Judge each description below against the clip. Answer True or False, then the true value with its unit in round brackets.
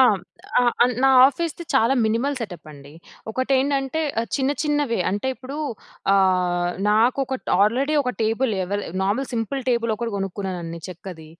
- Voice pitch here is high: True (230 Hz)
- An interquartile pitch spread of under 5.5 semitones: False (5.8 semitones)